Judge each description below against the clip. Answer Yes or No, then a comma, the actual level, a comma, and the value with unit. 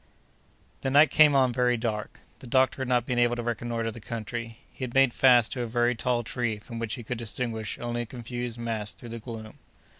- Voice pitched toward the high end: No, low, 120 Hz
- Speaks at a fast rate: Yes, fast, 220 wpm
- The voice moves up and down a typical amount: No, narrow, 1.6 semitones